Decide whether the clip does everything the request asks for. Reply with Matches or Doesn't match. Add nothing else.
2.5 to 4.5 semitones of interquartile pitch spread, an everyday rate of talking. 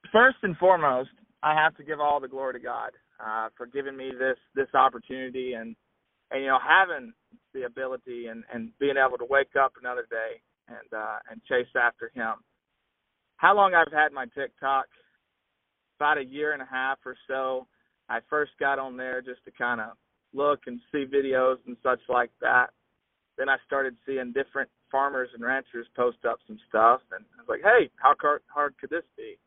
Matches